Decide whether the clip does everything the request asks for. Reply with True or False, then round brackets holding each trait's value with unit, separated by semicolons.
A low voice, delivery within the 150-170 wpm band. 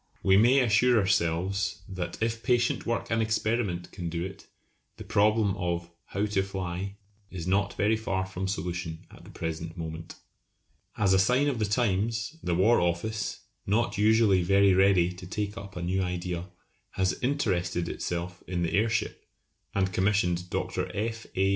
True (95 Hz; 165 wpm)